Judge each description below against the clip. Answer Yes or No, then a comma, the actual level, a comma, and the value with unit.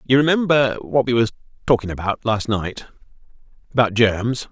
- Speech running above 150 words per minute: No, average, 145 wpm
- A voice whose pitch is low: Yes, low, 120 Hz